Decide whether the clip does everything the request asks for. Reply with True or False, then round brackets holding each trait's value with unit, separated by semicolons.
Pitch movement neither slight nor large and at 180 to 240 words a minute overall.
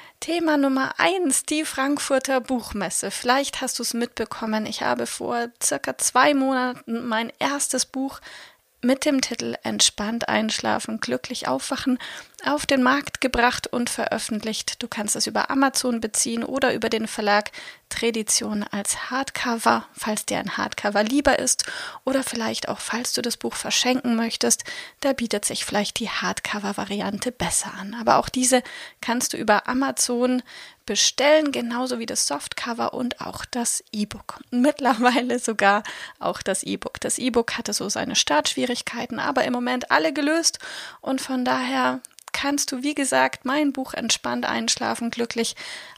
False (3.2 semitones; 150 wpm)